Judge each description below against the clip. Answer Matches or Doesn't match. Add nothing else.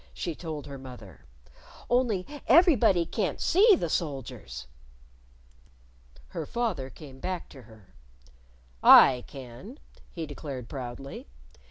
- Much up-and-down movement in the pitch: Matches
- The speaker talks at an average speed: Doesn't match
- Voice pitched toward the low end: Doesn't match